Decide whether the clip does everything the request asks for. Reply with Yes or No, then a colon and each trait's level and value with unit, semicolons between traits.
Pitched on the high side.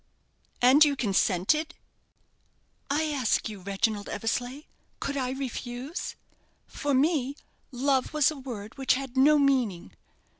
Yes: very high, 265 Hz